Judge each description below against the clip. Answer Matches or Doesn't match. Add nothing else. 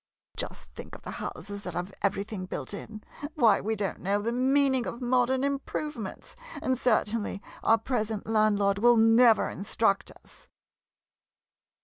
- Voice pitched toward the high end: Matches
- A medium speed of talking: Matches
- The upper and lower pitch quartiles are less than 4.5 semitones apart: Matches